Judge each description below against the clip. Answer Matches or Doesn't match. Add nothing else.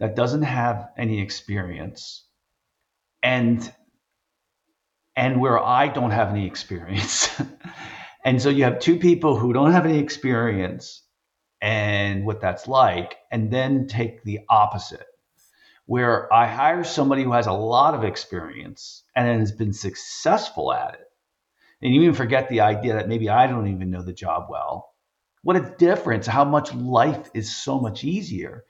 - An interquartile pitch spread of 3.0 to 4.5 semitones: Matches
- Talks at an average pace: Matches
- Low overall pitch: Matches